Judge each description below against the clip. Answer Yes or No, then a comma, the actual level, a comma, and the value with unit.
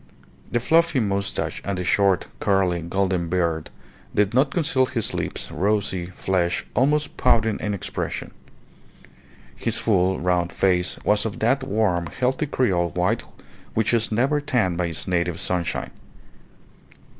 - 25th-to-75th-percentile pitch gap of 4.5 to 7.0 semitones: Yes, average, 5.1 semitones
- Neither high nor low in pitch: No, low, 100 Hz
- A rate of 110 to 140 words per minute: Yes, slow, 135 wpm